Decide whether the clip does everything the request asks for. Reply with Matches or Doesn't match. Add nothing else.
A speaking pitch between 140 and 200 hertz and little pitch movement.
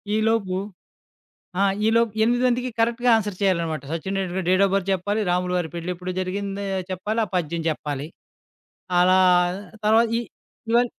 Doesn't match